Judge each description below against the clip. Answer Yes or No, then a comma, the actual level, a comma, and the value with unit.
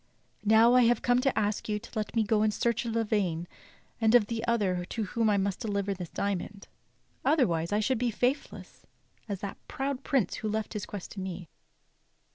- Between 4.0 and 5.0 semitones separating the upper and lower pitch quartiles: No, average, 2.8 semitones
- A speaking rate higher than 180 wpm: Yes, average, 200 wpm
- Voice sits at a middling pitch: No, high, 215 Hz